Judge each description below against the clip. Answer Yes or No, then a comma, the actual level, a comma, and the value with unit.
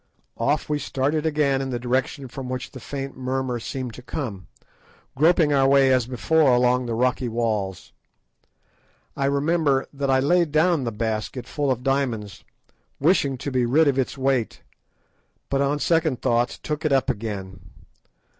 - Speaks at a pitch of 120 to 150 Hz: Yes, low, 135 Hz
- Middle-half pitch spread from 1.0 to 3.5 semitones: Yes, average, 2.7 semitones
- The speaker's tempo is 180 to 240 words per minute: No, average, 165 wpm